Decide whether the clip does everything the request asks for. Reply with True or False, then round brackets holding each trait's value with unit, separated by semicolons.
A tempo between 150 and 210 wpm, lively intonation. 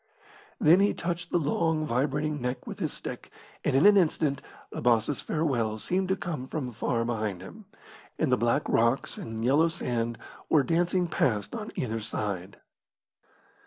True (160 wpm; 6.1 semitones)